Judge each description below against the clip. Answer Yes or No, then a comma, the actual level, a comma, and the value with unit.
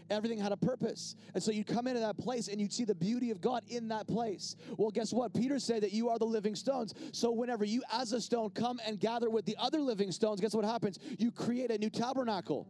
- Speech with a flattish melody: Yes, narrow, 2.2 semitones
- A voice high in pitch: Yes, high, 225 Hz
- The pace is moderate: No, fast, 255 wpm